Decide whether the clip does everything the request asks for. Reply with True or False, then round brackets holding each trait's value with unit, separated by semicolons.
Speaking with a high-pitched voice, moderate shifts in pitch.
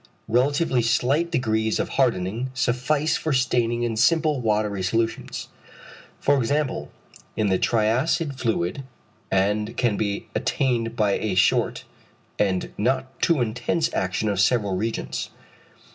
False (115 Hz; 3.8 semitones)